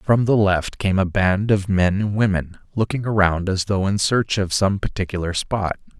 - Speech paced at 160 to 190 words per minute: No, average, 200 wpm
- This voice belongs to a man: Yes, male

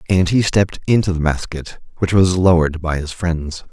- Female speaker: No, male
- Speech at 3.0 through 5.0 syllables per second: No, 5.2 syllables/s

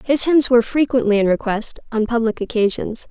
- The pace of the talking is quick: No, average, 175 wpm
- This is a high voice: Yes, high, 235 Hz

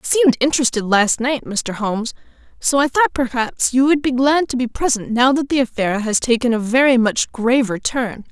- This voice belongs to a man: No, female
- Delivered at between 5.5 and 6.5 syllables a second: Yes, 5.7 syllables/s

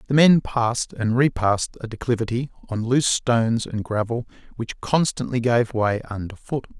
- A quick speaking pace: No, average, 160 wpm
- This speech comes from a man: Yes, male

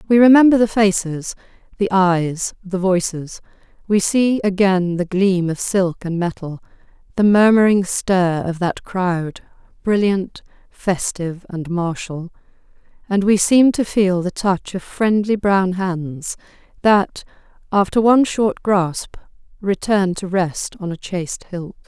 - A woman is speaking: Yes, female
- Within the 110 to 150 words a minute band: Yes, slow, 135 wpm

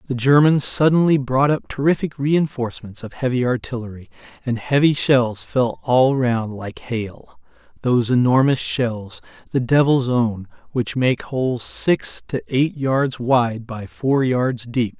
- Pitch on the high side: No, low, 125 Hz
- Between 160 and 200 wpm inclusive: No, average, 140 wpm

